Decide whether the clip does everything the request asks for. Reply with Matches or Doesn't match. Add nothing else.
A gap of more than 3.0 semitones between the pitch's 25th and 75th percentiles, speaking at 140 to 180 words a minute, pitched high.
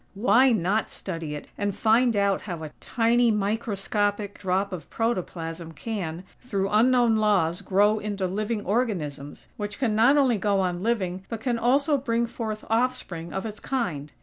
Matches